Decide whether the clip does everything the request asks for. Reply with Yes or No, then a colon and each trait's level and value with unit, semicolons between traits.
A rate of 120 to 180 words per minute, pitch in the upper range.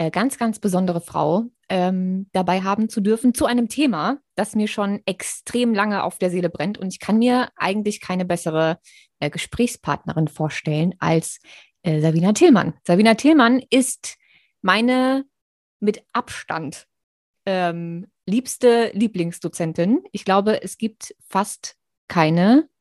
Yes: average, 130 wpm; high, 195 Hz